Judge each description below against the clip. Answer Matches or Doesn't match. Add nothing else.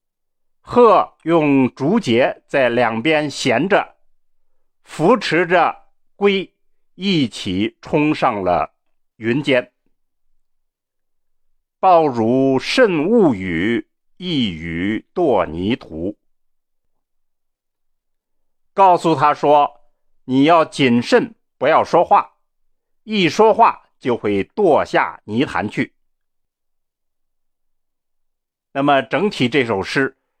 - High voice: Doesn't match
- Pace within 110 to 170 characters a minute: Matches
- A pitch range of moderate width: Doesn't match